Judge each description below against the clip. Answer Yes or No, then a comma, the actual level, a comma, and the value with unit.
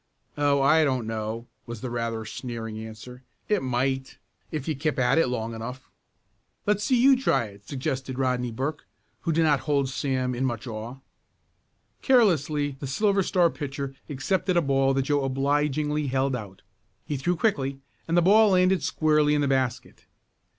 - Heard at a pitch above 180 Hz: No, low, 135 Hz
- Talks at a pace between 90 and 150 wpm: No, average, 170 wpm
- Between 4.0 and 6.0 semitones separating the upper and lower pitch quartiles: No, average, 3.6 semitones